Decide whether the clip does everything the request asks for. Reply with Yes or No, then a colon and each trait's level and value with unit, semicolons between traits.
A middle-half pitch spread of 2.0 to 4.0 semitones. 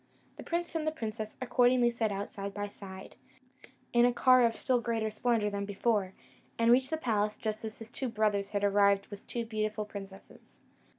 Yes: average, 2.9 semitones